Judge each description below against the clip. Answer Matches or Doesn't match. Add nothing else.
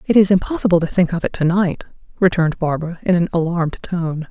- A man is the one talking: Doesn't match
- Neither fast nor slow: Doesn't match